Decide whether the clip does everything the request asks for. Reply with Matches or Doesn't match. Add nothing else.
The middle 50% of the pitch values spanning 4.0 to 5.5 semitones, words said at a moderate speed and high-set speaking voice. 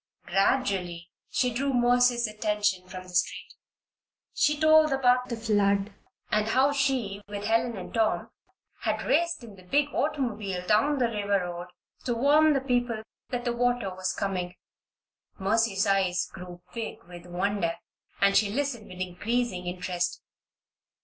Matches